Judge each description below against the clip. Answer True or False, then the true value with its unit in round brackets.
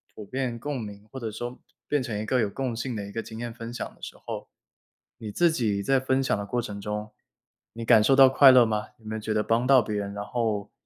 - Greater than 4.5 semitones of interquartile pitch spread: False (3.3 semitones)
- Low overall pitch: True (115 Hz)